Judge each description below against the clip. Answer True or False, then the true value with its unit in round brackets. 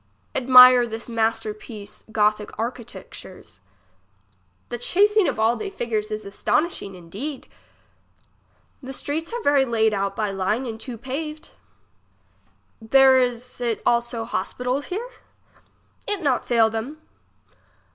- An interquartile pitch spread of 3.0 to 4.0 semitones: True (3.5 semitones)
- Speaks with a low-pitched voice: False (240 Hz)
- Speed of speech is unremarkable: False (120 wpm)